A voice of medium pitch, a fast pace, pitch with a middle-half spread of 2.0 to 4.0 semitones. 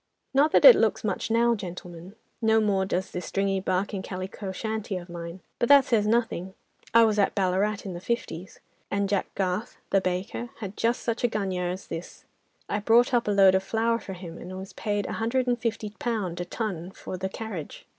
No: high, 200 Hz; fast, 210 wpm; average, 3.3 semitones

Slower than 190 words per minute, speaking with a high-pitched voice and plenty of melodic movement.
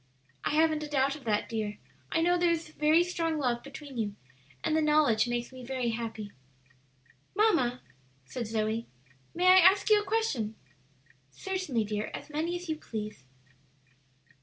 Yes: average, 160 wpm; very high, 285 Hz; wide, 6.7 semitones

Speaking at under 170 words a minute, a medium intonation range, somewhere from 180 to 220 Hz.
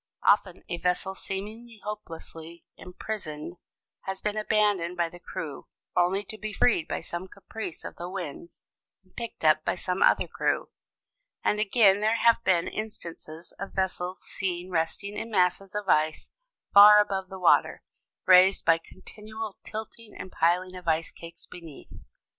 Yes: average, 155 wpm; average, 3.4 semitones; medium, 185 Hz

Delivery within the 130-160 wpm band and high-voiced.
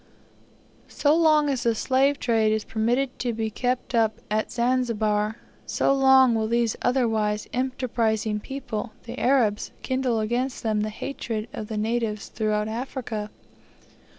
Yes: average, 140 wpm; high, 230 Hz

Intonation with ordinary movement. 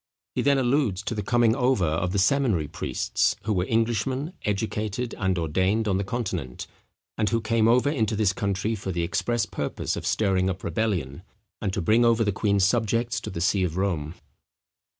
Yes: average, 3.7 semitones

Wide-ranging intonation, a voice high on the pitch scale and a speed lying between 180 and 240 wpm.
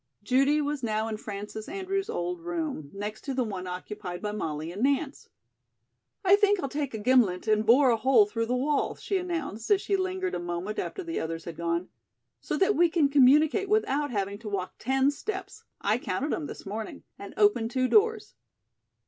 Yes: wide, 8.1 semitones; very high, 255 Hz; average, 195 wpm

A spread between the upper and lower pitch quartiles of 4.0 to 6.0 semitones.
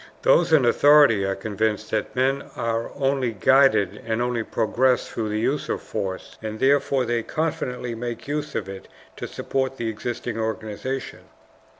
No: average, 3.6 semitones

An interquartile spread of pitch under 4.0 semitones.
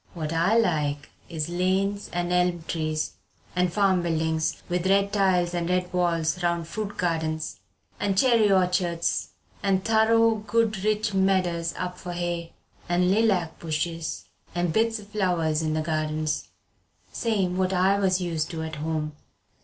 Yes: average, 3.2 semitones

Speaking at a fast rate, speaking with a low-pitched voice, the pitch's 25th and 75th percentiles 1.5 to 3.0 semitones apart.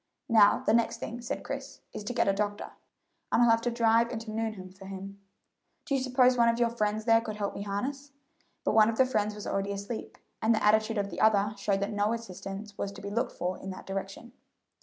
No: fast, 235 wpm; high, 215 Hz; narrow, 2.5 semitones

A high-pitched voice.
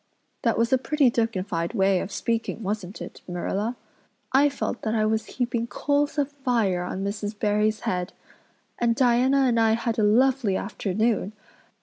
Yes: high, 225 Hz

